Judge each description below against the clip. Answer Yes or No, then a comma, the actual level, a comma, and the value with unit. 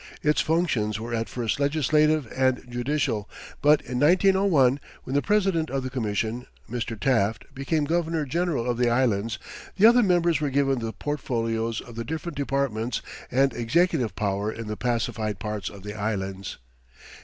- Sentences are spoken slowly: No, average, 160 wpm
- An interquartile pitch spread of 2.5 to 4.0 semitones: No, average, 5.2 semitones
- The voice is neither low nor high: No, low, 125 Hz